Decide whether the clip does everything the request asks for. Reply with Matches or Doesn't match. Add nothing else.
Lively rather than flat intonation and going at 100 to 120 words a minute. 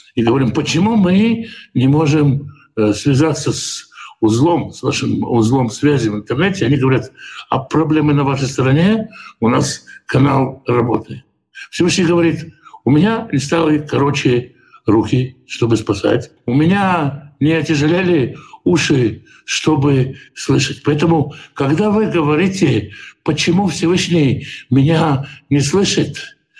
Doesn't match